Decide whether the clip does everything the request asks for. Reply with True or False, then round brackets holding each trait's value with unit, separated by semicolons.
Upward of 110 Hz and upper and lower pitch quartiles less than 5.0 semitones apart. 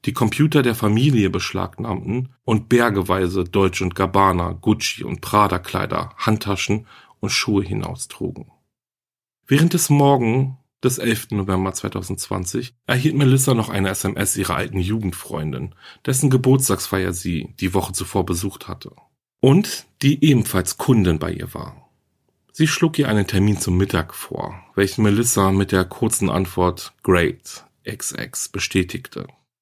False (100 Hz; 4.5 semitones)